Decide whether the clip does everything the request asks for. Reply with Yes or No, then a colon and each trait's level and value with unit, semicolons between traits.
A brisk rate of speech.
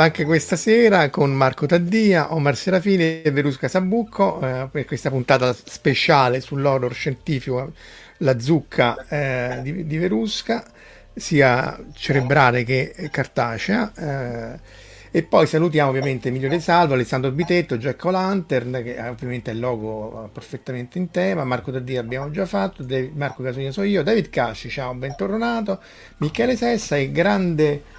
No: average, 140 wpm